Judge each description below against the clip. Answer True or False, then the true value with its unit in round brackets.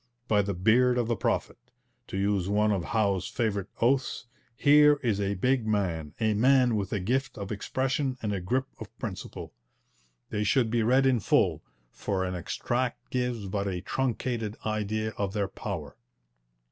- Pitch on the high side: False (110 Hz)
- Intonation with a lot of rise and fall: False (3.9 semitones)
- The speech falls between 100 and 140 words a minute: False (170 wpm)